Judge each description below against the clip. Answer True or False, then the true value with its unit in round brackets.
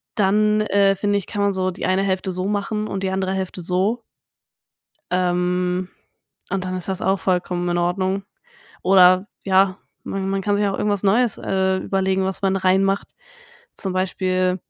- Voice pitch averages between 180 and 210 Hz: True (190 Hz)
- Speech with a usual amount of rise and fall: False (1.2 semitones)